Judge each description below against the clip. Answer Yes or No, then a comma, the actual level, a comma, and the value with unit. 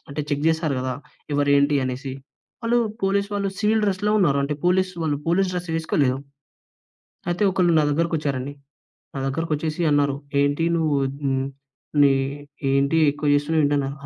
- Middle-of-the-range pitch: Yes, medium, 150 Hz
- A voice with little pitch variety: No, average, 3.7 semitones